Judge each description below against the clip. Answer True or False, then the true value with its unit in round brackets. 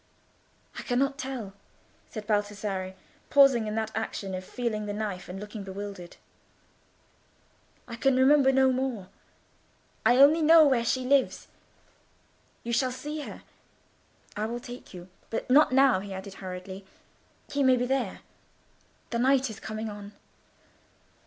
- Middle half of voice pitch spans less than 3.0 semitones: False (4.4 semitones)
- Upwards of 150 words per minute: False (140 wpm)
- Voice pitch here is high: True (235 Hz)